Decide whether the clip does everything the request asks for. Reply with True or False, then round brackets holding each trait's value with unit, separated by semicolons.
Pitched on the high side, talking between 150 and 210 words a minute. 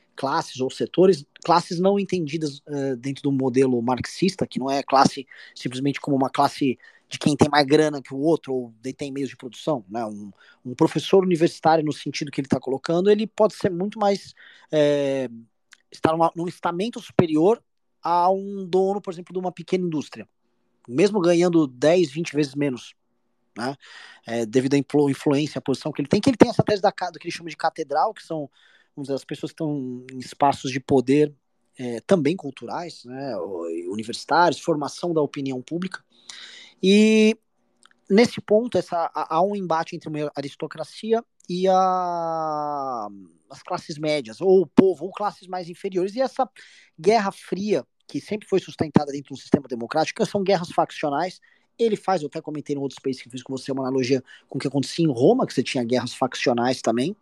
False (155 Hz; 180 wpm)